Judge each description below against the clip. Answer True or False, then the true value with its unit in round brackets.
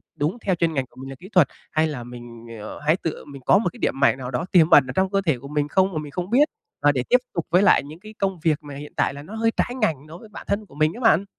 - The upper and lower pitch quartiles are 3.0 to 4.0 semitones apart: False (5.3 semitones)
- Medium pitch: True (155 Hz)